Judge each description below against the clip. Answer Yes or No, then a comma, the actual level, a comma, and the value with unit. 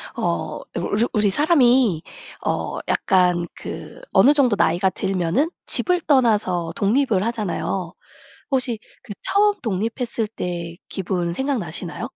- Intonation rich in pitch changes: Yes, wide, 6.3 semitones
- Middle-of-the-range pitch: No, high, 210 Hz